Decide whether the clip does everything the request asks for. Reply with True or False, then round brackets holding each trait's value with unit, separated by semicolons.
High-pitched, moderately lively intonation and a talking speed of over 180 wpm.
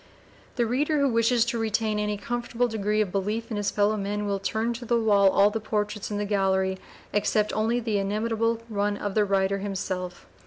False (210 Hz; 2.2 semitones; 200 wpm)